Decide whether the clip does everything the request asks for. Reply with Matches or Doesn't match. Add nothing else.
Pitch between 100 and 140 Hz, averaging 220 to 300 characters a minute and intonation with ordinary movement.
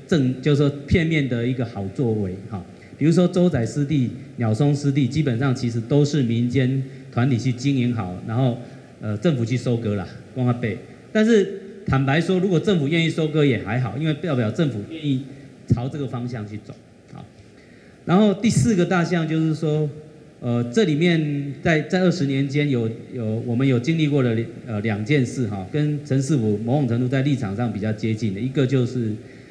Matches